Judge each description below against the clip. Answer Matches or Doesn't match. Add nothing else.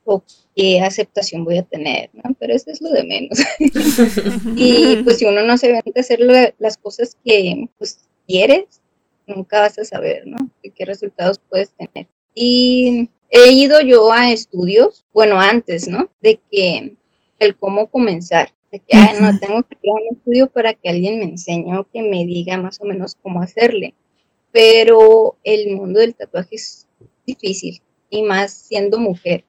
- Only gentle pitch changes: Doesn't match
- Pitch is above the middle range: Matches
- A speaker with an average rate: Matches